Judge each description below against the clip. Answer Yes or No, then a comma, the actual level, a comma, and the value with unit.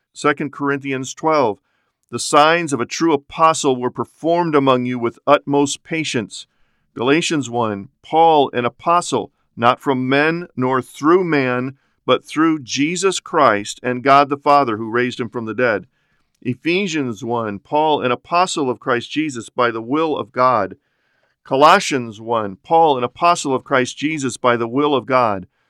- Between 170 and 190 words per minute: No, average, 155 wpm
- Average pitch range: Yes, average, 4.0 semitones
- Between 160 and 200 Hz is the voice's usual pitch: No, low, 135 Hz